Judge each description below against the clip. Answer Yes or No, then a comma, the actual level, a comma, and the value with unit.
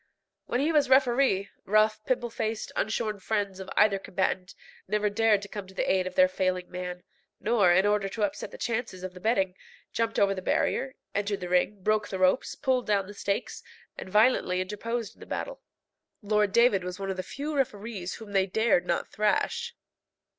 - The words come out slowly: No, average, 195 wpm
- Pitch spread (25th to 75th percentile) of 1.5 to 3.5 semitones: Yes, average, 3.2 semitones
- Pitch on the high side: Yes, high, 205 Hz